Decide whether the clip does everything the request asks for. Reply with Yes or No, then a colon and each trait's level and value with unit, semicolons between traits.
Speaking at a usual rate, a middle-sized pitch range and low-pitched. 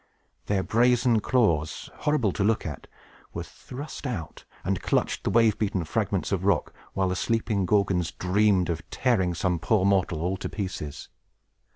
Yes: average, 160 wpm; average, 4.1 semitones; low, 100 Hz